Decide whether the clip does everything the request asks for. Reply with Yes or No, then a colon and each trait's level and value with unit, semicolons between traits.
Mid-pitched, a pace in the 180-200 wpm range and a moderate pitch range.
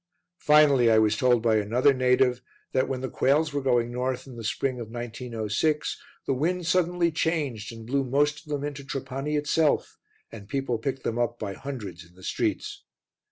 No: low, 130 Hz; average, 185 wpm; average, 3.8 semitones